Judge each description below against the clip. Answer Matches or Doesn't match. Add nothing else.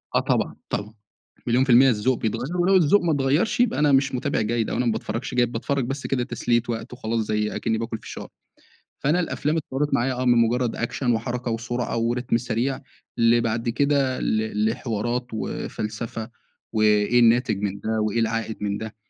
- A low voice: Matches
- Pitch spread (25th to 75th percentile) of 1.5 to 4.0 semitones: Matches